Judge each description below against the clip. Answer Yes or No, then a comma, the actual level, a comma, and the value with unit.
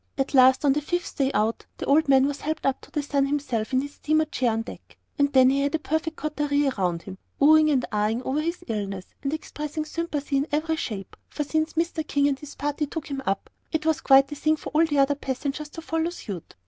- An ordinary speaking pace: No, fast, 245 wpm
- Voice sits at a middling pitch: No, very high, 285 Hz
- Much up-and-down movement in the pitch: No, average, 2.8 semitones